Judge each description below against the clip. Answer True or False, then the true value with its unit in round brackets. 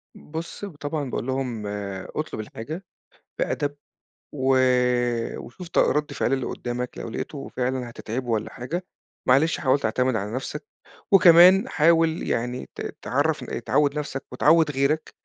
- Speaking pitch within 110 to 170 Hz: True (140 Hz)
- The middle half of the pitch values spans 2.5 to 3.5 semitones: False (4.2 semitones)